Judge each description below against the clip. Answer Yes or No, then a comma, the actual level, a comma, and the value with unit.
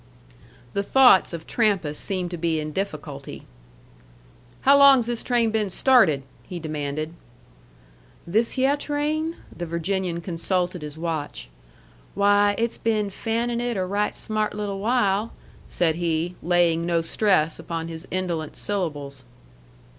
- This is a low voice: No, medium, 185 Hz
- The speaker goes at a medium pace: No, slow, 130 wpm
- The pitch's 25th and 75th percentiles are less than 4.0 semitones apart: No, average, 5.2 semitones